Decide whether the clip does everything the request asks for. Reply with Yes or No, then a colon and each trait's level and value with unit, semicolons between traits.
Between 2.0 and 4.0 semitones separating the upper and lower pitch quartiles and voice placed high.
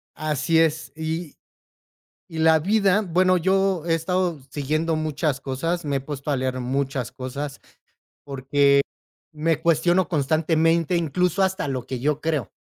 No: average, 3.5 semitones; medium, 155 Hz